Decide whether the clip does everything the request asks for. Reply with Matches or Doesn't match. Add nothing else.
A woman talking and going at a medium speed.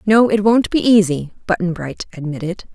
Matches